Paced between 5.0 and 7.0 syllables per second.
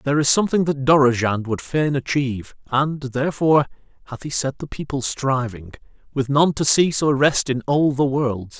Yes: 5.2 syllables/s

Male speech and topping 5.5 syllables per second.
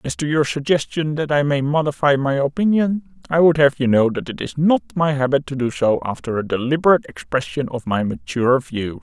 Yes: male; 5.7 syllables/s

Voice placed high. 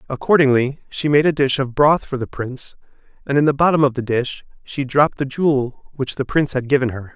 No: low, 135 Hz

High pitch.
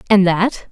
Yes: high, 195 Hz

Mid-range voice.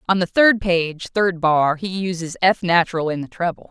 Yes: medium, 175 Hz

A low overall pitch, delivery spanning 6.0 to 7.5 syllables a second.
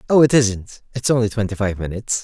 Yes: low, 110 Hz; 6.3 syllables/s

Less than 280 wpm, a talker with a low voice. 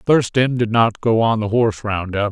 Yes: fast, 205 wpm; low, 115 Hz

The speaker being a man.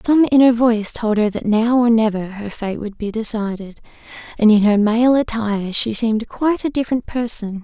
No: female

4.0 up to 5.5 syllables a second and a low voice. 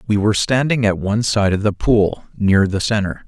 Yes: 5.4 syllables/s; low, 105 Hz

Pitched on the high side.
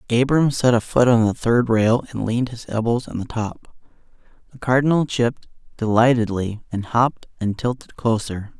No: low, 120 Hz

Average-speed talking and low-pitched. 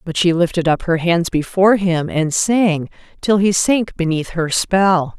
No: average, 185 wpm; medium, 180 Hz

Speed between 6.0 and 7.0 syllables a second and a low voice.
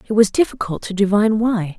No: 6.3 syllables/s; high, 210 Hz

